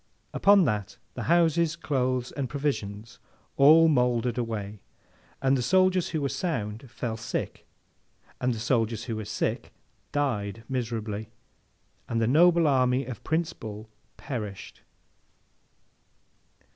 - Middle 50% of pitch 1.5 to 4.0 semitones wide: No, average, 5.2 semitones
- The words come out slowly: Yes, slow, 120 wpm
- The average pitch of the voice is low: Yes, low, 125 Hz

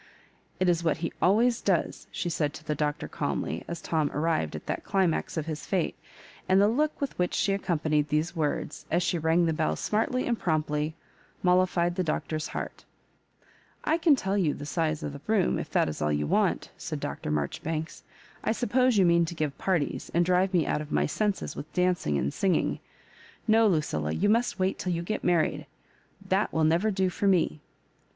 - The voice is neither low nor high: Yes, medium, 170 Hz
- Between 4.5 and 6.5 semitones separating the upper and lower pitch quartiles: No, average, 4.1 semitones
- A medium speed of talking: No, fast, 210 wpm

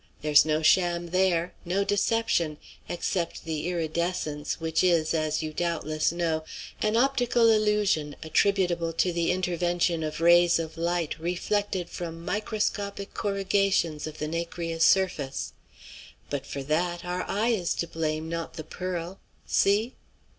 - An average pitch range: Yes, average, 3.1 semitones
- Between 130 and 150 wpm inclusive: Yes, slow, 135 wpm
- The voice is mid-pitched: Yes, medium, 170 Hz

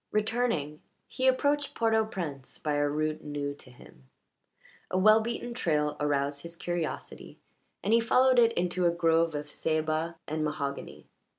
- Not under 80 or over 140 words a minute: No, average, 160 wpm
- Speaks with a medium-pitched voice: Yes, medium, 165 Hz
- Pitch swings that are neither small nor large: No, wide, 7.0 semitones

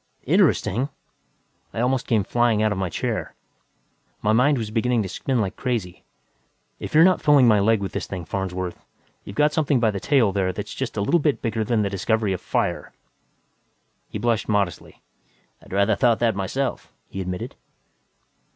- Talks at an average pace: Yes, average, 180 wpm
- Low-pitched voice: Yes, low, 110 Hz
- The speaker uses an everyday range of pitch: Yes, average, 4.1 semitones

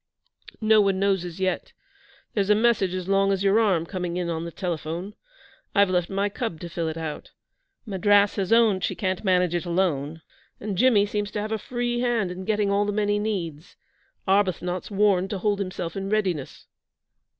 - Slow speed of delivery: No, average, 195 wpm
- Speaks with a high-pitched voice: Yes, high, 195 Hz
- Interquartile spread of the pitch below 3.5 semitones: Yes, narrow, 2.6 semitones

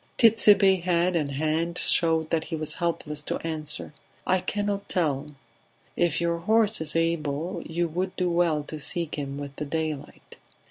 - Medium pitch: Yes, medium, 165 Hz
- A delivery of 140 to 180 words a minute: Yes, average, 165 wpm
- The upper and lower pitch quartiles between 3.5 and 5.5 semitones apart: No, average, 2.8 semitones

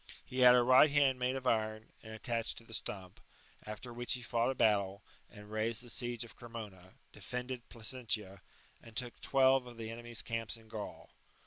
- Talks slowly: No, average, 190 wpm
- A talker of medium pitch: No, low, 115 Hz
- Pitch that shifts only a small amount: Yes, narrow, 2.3 semitones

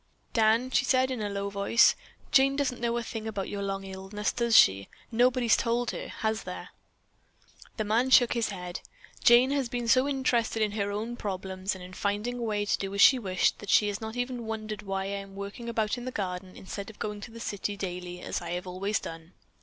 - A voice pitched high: Yes, high, 215 Hz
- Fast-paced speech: Yes, fast, 225 wpm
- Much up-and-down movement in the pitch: No, average, 3.4 semitones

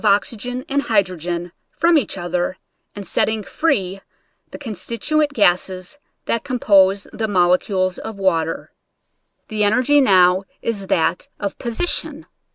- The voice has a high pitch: Yes, high, 200 Hz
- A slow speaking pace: Yes, slow, 125 wpm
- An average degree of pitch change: Yes, average, 4.3 semitones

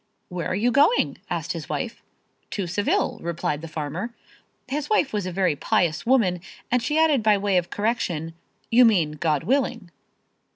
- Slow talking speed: No, average, 170 wpm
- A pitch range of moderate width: No, wide, 6.3 semitones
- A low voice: No, high, 200 Hz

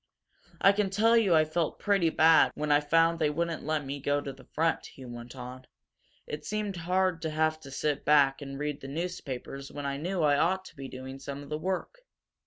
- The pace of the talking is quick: Yes, fast, 220 wpm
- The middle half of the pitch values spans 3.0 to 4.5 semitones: Yes, average, 3.6 semitones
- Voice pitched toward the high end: No, medium, 150 Hz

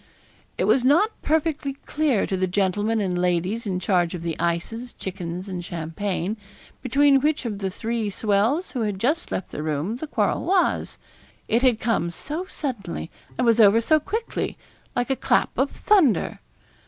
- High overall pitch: Yes, high, 220 Hz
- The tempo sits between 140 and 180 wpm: Yes, average, 170 wpm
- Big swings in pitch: Yes, wide, 7.0 semitones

